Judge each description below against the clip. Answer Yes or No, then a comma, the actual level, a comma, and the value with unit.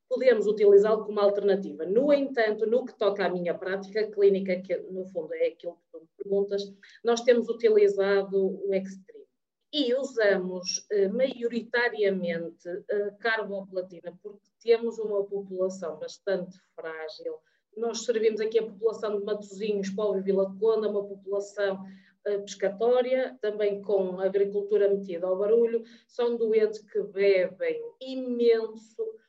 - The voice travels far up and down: No, average, 3.1 semitones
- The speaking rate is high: No, average, 135 wpm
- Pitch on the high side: Yes, high, 205 Hz